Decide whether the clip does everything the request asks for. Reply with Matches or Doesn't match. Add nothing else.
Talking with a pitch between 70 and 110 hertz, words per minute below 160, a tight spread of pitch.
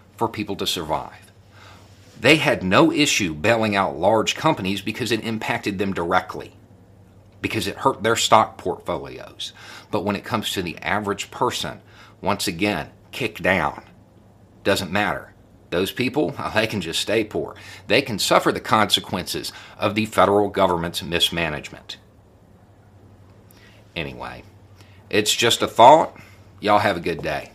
Matches